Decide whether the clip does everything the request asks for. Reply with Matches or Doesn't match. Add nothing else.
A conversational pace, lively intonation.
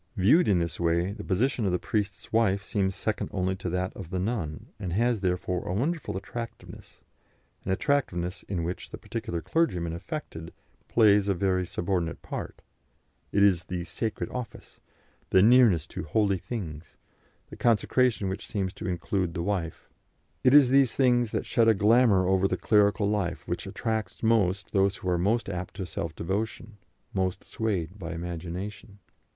Doesn't match